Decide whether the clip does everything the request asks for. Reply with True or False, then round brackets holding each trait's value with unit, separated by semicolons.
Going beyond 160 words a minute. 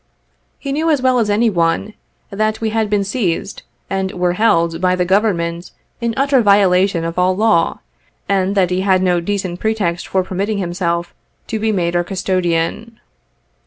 True (170 wpm)